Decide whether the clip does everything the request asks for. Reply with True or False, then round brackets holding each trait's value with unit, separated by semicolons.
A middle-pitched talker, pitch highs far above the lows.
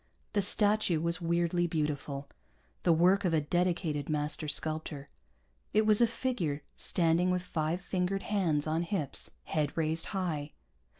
False (170 Hz; 3.1 semitones)